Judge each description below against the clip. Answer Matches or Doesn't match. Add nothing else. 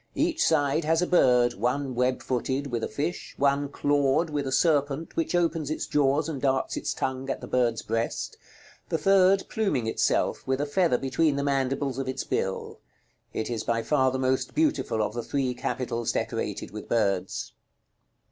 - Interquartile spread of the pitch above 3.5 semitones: Doesn't match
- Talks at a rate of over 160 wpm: Matches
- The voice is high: Doesn't match